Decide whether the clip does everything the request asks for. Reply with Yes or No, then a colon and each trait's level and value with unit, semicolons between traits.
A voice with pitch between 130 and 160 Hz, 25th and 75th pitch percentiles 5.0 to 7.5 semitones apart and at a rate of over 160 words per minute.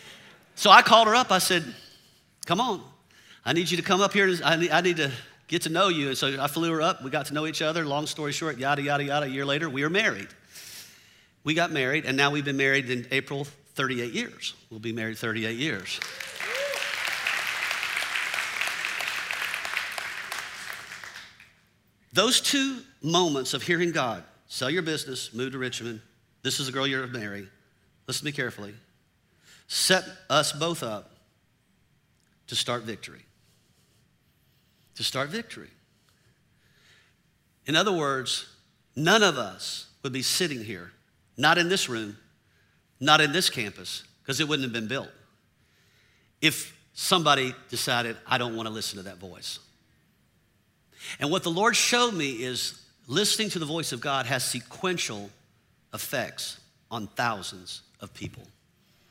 No: low, 135 Hz; wide, 5.6 semitones; average, 155 wpm